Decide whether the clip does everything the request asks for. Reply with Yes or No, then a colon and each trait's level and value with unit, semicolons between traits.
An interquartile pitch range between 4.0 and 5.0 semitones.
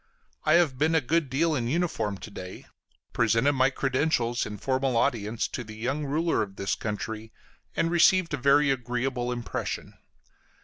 Yes: average, 4.7 semitones